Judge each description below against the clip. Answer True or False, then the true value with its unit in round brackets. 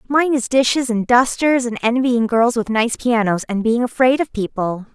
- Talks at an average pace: True (195 wpm)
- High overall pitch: True (240 Hz)